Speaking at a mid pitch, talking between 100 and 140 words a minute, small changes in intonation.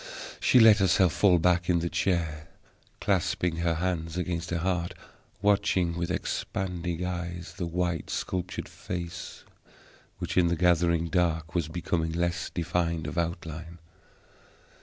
No: very low, 85 Hz; slow, 135 wpm; narrow, 1.3 semitones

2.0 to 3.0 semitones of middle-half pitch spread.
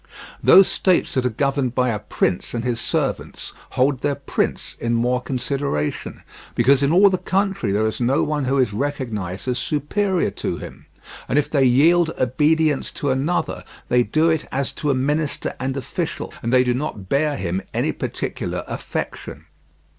No: average, 3.5 semitones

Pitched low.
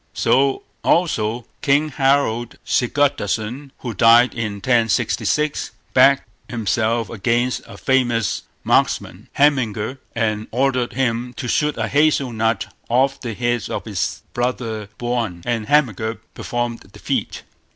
Yes: low, 120 Hz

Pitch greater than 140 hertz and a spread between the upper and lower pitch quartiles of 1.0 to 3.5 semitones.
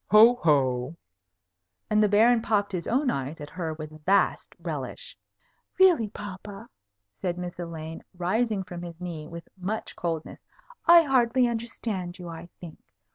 No: medium, 185 Hz; average, 5.2 semitones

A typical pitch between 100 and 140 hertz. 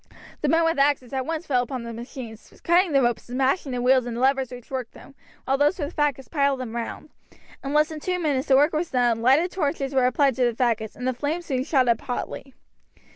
No: very high, 265 Hz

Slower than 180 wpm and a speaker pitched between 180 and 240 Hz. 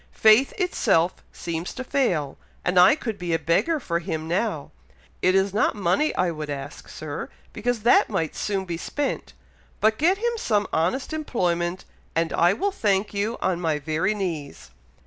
Yes: average, 170 wpm; high, 190 Hz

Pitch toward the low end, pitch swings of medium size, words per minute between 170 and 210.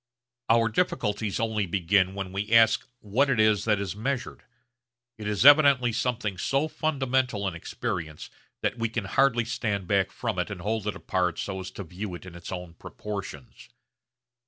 Yes: low, 105 Hz; average, 3.8 semitones; average, 175 wpm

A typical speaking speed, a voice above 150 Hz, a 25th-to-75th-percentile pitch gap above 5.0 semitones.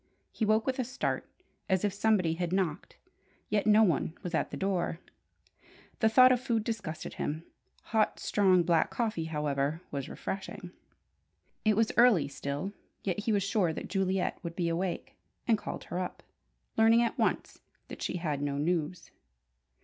No: average, 165 wpm; high, 190 Hz; average, 4.7 semitones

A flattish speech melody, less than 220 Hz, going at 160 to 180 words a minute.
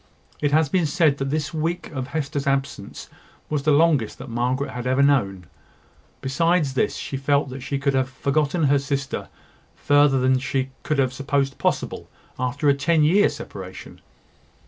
Yes: narrow, 2.2 semitones; medium, 140 Hz; average, 165 wpm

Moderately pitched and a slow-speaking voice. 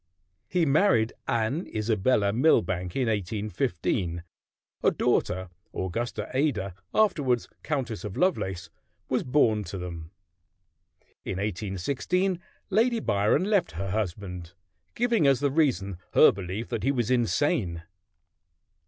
No: low, 110 Hz; slow, 115 wpm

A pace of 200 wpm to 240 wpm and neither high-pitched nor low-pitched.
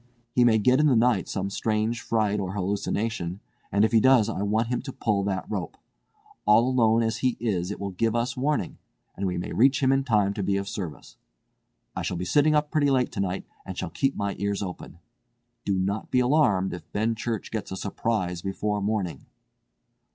No: fast, 205 wpm; low, 105 Hz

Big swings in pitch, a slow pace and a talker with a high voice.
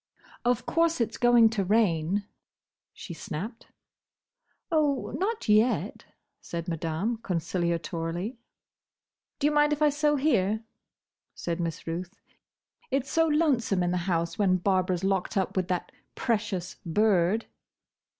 Yes: wide, 5.8 semitones; slow, 125 wpm; high, 200 Hz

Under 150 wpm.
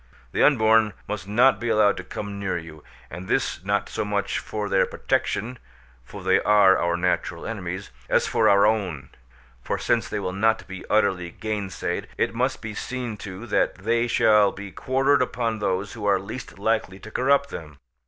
No: average, 185 wpm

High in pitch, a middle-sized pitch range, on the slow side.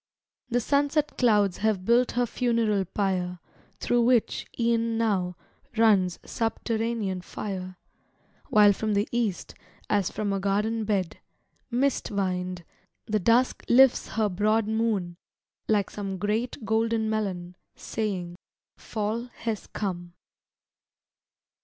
Yes: high, 215 Hz; average, 3.1 semitones; slow, 115 wpm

